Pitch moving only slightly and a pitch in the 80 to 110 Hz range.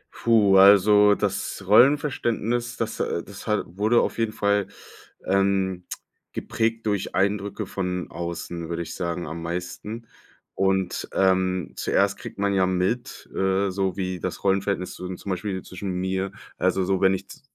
Yes: narrow, 1.9 semitones; very low, 95 Hz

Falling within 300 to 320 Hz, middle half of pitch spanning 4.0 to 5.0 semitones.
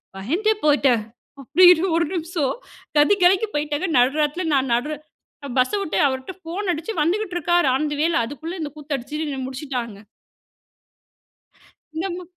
Yes: very high, 305 Hz; average, 4.5 semitones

